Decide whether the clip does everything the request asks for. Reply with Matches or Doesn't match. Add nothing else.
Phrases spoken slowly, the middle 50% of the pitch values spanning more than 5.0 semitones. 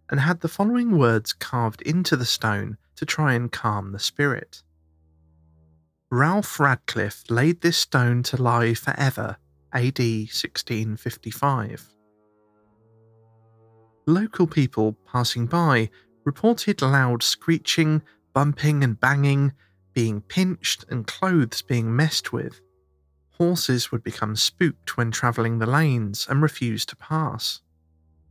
Matches